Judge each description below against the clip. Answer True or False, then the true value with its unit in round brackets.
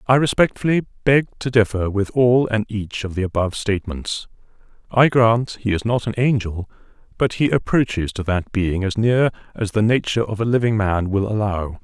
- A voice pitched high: False (110 Hz)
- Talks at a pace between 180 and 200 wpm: True (190 wpm)